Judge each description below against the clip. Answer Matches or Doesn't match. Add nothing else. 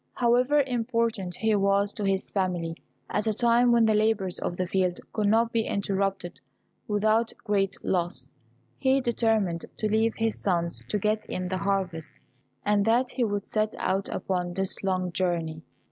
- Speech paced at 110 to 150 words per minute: Doesn't match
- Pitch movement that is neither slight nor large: Matches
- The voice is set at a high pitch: Matches